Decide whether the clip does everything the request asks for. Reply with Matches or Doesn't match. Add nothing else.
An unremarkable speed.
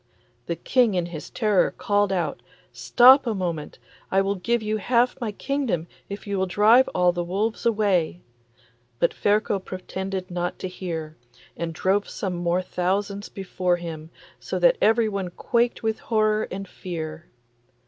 Matches